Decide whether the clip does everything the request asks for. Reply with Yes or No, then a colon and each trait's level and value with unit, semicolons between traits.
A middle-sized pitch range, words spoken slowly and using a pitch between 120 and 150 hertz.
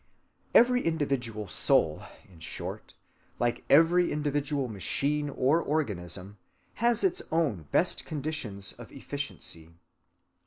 No: wide, 7.6 semitones; slow, 105 wpm; medium, 140 Hz